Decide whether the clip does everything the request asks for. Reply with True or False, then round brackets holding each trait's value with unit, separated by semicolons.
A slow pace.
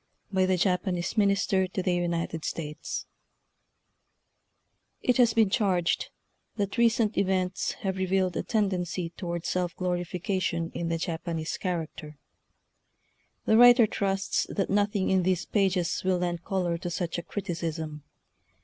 True (120 wpm)